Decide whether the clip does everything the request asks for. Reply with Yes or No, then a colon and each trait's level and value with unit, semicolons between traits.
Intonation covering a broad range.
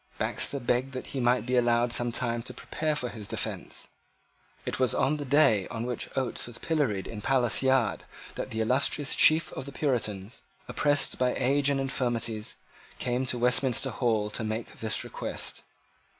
No: narrow, 2.6 semitones